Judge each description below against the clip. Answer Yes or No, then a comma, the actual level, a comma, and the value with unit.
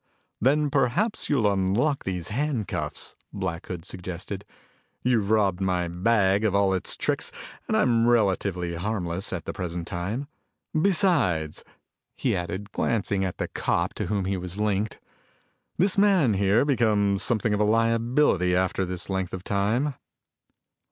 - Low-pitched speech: Yes, low, 100 Hz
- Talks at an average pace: Yes, average, 145 wpm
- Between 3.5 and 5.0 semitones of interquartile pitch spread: Yes, average, 4.2 semitones